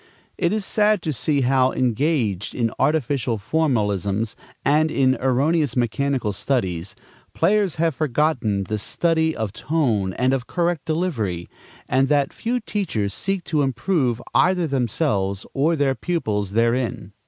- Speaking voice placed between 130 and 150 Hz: Yes, low, 135 Hz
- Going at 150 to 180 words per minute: No, slow, 135 wpm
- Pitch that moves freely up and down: Yes, wide, 6.3 semitones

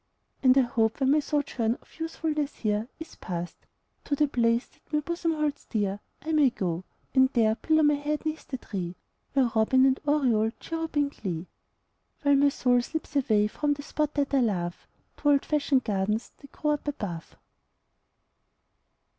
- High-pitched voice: Yes, very high, 270 Hz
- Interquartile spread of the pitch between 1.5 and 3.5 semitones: No, average, 5.1 semitones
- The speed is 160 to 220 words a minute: Yes, average, 175 wpm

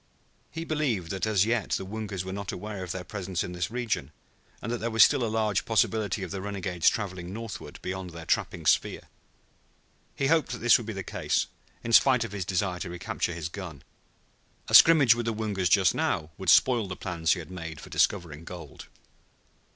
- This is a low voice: Yes, low, 100 Hz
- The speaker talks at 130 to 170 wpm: No, fast, 205 wpm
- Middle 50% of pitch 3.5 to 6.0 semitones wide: Yes, average, 4.1 semitones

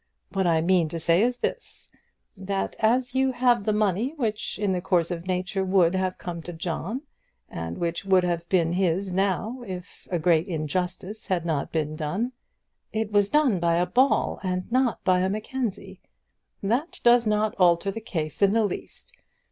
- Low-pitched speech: No, high, 190 Hz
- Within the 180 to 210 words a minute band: Yes, average, 185 wpm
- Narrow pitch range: No, average, 4.0 semitones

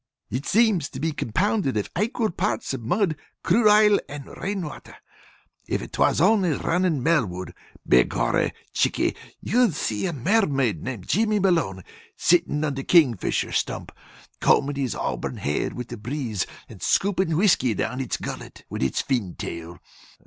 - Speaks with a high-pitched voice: No, medium, 150 Hz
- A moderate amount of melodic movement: No, wide, 8.1 semitones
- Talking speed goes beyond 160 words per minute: No, average, 155 wpm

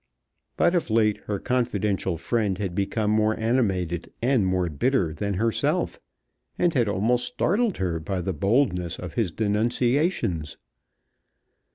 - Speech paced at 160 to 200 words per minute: No, slow, 135 wpm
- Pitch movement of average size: Yes, average, 4.7 semitones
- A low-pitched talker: Yes, low, 105 Hz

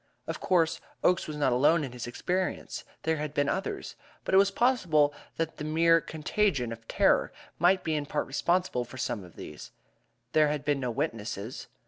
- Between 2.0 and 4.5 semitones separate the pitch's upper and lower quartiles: No, average, 5.2 semitones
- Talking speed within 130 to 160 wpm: No, average, 185 wpm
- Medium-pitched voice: Yes, medium, 150 Hz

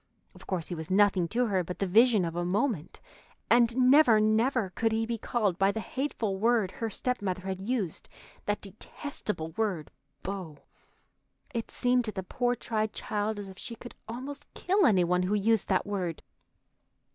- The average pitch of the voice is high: Yes, high, 210 Hz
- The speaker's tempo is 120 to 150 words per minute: No, average, 180 wpm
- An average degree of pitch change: Yes, average, 4.0 semitones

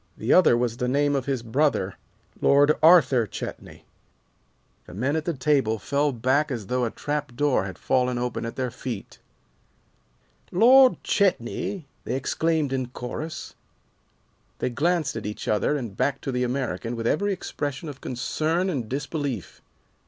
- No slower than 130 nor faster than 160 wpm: Yes, average, 150 wpm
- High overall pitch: No, low, 135 Hz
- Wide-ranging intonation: No, average, 3.9 semitones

